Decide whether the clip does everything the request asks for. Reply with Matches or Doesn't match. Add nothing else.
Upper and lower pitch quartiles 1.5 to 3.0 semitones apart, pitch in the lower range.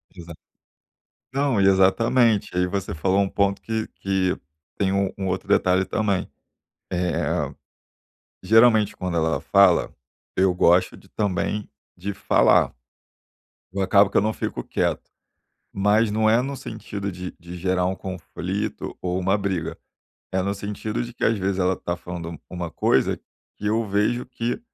Matches